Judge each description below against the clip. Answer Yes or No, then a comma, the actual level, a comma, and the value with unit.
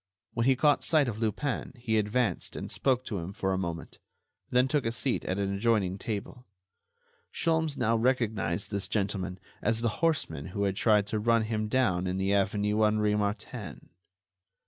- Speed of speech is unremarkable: Yes, average, 175 wpm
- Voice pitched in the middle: No, low, 110 Hz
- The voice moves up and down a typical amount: Yes, average, 3.7 semitones